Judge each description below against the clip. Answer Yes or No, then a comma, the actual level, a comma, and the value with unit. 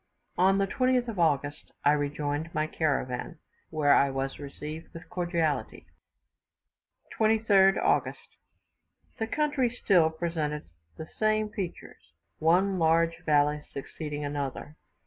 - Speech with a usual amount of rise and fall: Yes, average, 4.8 semitones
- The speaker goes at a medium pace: No, slow, 115 wpm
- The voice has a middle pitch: Yes, medium, 160 Hz